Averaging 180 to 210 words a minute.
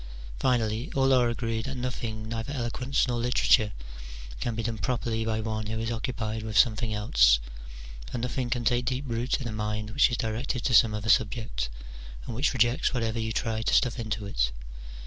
Yes: average, 190 wpm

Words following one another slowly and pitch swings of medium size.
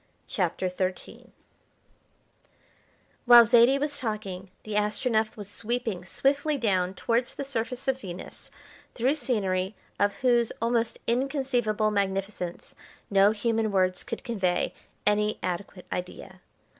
Yes: slow, 115 wpm; average, 4.0 semitones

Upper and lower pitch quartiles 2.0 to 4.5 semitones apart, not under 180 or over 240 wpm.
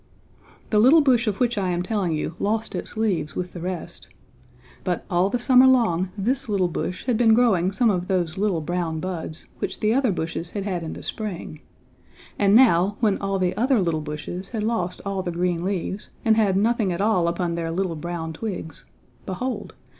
Yes: average, 4.1 semitones; average, 200 wpm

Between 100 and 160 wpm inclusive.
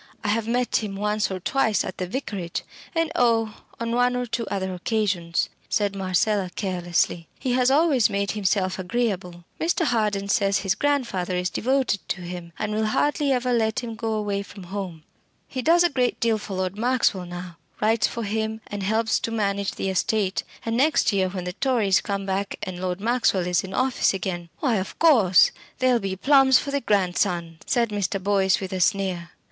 No: average, 195 wpm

